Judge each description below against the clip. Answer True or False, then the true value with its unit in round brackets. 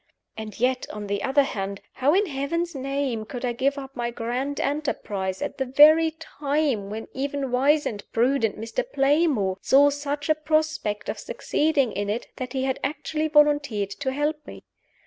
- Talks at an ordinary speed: True (175 wpm)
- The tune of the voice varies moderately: True (4.3 semitones)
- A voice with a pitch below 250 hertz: False (275 Hz)